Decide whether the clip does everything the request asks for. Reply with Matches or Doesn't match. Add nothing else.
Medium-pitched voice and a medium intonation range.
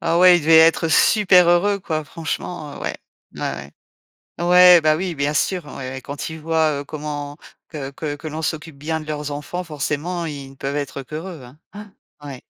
Matches